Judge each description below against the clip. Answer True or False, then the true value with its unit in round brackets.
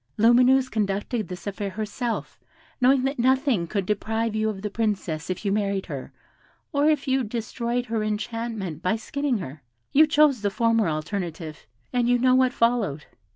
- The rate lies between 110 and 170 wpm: True (165 wpm)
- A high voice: True (220 Hz)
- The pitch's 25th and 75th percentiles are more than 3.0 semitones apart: True (4.1 semitones)